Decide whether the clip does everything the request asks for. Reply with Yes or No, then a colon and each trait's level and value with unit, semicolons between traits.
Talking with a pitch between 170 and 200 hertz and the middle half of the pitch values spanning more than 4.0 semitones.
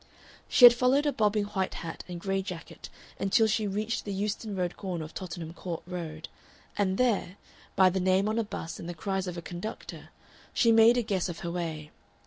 No: high, 190 Hz; average, 3.6 semitones